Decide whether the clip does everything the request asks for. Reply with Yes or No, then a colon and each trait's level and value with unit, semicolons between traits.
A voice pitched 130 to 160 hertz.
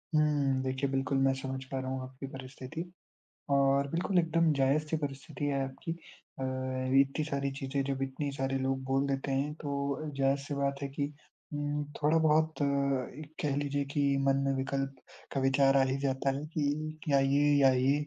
Yes: medium, 140 Hz